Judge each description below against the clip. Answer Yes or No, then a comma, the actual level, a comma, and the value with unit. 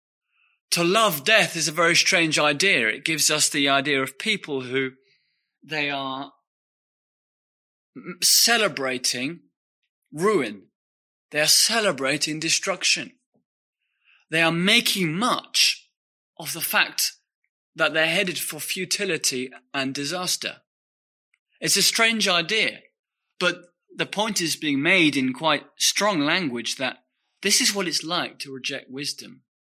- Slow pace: Yes, slow, 125 wpm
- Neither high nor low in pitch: Yes, medium, 165 Hz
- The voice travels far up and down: Yes, wide, 6.2 semitones